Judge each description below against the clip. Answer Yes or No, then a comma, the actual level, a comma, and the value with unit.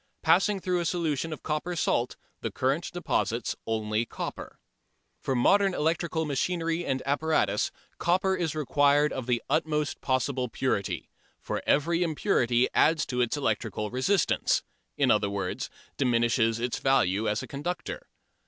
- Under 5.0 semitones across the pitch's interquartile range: No, wide, 5.6 semitones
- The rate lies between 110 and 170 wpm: Yes, average, 140 wpm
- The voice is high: No, medium, 145 Hz